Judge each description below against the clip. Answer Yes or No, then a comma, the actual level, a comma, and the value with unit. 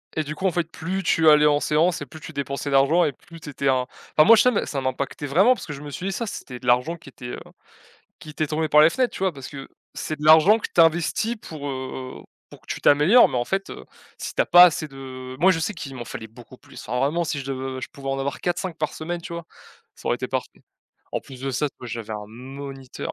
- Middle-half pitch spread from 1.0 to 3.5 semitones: No, average, 4.1 semitones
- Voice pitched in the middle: Yes, medium, 150 Hz